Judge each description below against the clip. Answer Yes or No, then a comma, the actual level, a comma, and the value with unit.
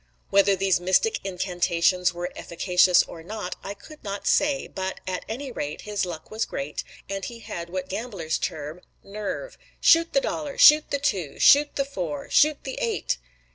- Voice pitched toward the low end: No, high, 195 Hz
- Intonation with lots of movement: Yes, wide, 6.1 semitones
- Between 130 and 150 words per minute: No, average, 175 wpm